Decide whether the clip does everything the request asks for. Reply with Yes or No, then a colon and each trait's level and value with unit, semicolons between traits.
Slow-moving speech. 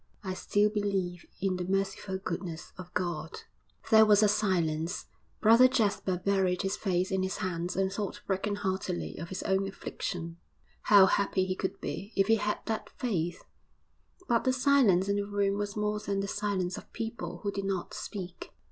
No: average, 175 wpm